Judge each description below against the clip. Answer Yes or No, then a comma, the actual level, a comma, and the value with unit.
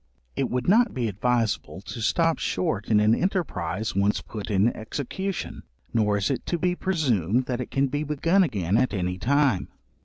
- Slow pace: No, average, 180 wpm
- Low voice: Yes, low, 120 Hz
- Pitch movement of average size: No, wide, 6.4 semitones